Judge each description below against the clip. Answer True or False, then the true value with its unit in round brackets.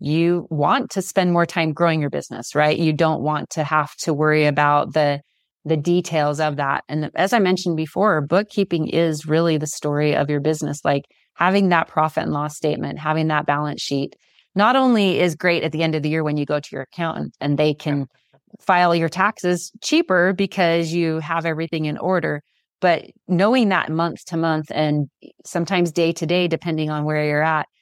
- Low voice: False (160 Hz)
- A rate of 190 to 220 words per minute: True (200 wpm)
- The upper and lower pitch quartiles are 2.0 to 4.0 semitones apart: True (2.6 semitones)